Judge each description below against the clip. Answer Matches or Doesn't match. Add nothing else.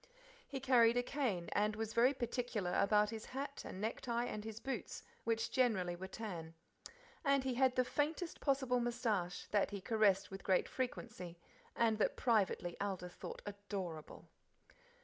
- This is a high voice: Matches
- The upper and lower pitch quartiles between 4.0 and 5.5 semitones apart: Matches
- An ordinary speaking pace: Matches